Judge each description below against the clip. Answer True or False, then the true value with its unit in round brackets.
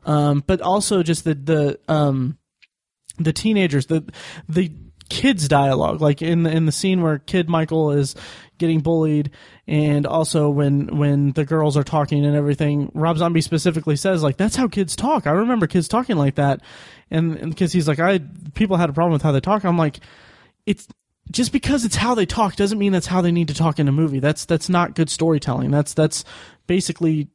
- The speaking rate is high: False (195 wpm)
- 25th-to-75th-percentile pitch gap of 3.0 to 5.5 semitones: True (3.4 semitones)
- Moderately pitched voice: True (160 Hz)